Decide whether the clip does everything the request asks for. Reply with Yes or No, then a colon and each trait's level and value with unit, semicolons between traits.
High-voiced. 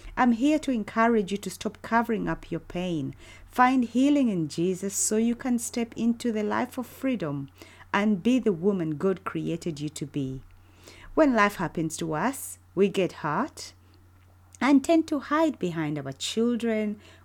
Yes: high, 195 Hz